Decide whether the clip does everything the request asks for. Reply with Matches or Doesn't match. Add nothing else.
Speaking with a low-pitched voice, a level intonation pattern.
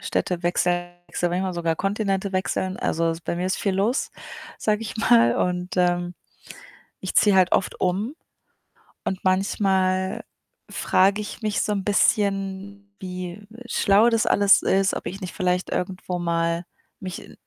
Doesn't match